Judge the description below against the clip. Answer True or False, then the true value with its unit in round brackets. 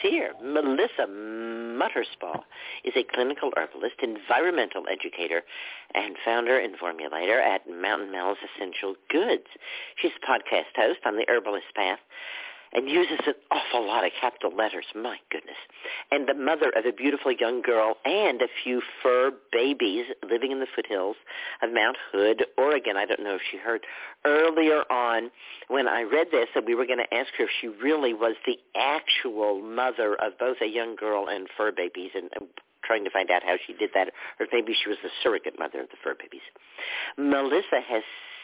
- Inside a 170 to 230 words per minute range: True (180 wpm)